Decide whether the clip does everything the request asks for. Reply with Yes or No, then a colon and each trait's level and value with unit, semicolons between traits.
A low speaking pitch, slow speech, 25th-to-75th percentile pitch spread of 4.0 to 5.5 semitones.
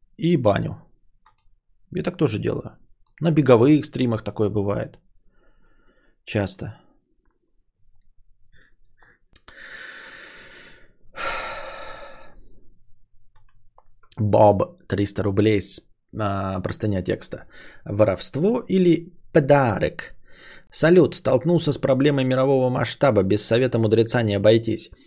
Yes: low, 110 Hz; slow, 80 wpm; average, 4.7 semitones